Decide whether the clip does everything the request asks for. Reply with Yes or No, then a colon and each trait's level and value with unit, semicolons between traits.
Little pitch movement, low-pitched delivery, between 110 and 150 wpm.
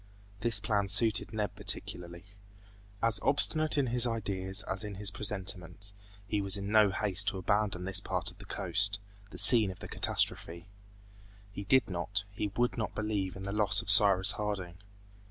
No: narrow, 2.0 semitones; low, 100 Hz; average, 170 wpm